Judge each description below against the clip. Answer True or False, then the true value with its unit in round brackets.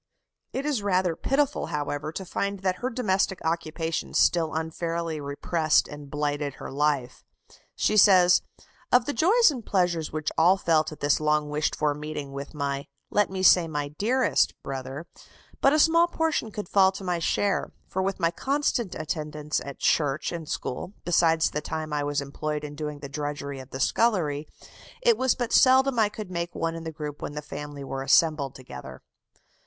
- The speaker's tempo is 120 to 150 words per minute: False (180 wpm)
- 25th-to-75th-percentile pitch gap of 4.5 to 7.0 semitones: True (4.9 semitones)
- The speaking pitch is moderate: True (160 Hz)